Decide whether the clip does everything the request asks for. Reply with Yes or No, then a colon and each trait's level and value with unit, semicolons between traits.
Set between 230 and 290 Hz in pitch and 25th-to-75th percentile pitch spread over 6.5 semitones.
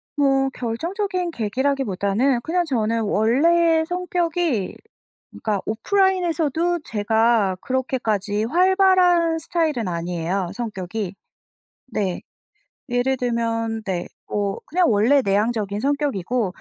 Yes: high, 245 Hz; wide, 7.8 semitones